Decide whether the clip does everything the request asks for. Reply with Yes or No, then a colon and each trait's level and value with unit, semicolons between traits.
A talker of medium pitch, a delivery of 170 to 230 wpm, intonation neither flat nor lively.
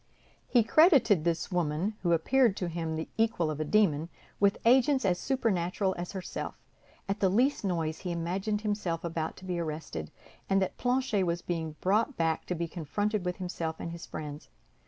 Yes: medium, 180 Hz; average, 180 wpm; average, 4.2 semitones